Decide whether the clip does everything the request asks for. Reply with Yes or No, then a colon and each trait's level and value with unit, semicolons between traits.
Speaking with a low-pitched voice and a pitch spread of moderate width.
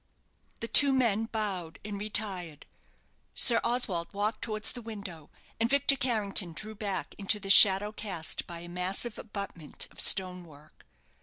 No: high, 205 Hz; average, 3.6 semitones